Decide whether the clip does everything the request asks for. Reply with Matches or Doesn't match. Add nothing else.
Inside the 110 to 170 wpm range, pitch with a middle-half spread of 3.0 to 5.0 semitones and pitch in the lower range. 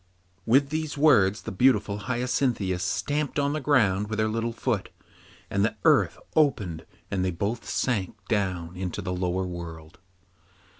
Doesn't match